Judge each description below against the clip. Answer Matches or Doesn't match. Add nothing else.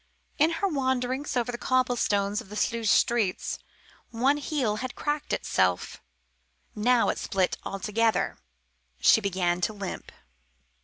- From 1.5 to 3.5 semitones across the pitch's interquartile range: Doesn't match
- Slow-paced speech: Matches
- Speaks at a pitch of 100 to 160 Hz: Doesn't match